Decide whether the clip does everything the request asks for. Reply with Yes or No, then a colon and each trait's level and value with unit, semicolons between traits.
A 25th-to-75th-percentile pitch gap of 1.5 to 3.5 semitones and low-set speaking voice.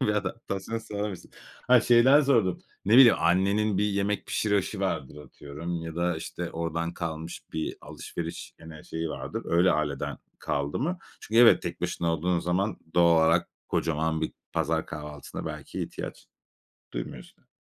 No: average, 4.3 semitones; very low, 85 Hz